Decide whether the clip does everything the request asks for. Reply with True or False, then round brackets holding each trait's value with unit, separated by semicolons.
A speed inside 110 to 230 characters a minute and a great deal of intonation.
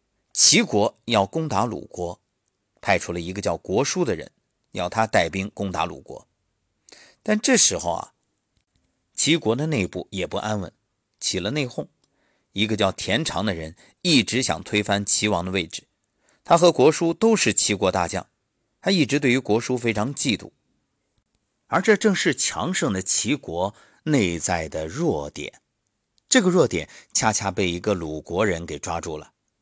True (225 characters per minute; 5.9 semitones)